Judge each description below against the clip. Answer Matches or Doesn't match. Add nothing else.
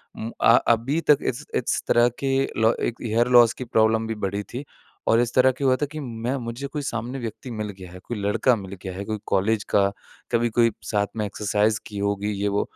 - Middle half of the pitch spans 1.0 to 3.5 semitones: Matches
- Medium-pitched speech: Doesn't match